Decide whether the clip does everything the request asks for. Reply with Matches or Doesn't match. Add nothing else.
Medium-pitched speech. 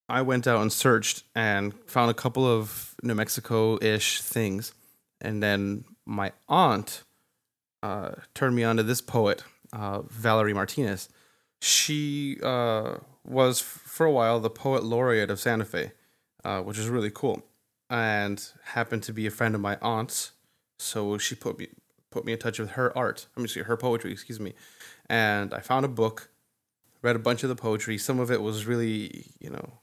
Doesn't match